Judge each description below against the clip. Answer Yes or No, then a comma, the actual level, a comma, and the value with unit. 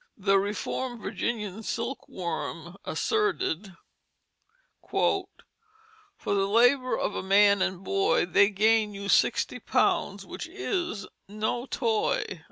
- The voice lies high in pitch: Yes, high, 210 Hz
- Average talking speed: No, slow, 110 wpm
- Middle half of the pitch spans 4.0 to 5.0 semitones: Yes, average, 4.3 semitones